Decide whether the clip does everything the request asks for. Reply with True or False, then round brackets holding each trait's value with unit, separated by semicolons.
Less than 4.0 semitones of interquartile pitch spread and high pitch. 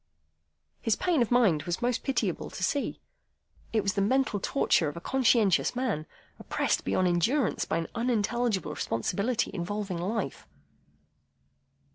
False (5.6 semitones; 215 Hz)